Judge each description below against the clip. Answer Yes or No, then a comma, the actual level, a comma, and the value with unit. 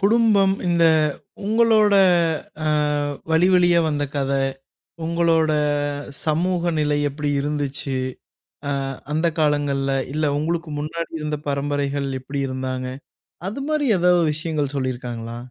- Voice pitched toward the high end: No, medium, 155 Hz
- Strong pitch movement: No, average, 3.7 semitones